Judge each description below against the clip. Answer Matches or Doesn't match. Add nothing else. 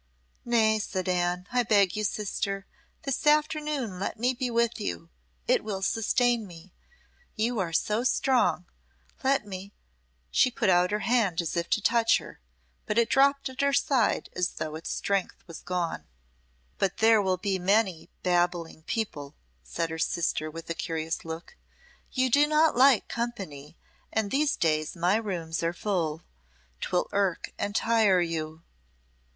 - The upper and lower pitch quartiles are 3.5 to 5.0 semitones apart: Doesn't match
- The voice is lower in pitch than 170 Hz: Doesn't match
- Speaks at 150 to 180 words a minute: Matches